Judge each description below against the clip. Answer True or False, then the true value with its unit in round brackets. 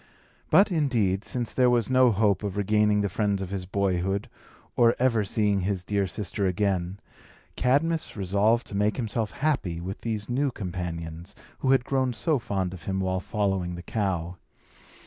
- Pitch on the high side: False (100 Hz)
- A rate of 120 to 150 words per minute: False (165 wpm)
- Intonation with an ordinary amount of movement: True (4.0 semitones)